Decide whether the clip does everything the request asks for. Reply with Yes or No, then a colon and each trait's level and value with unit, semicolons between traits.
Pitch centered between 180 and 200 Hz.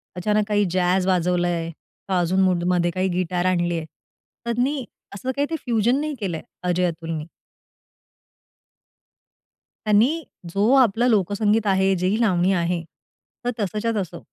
Yes: high, 190 Hz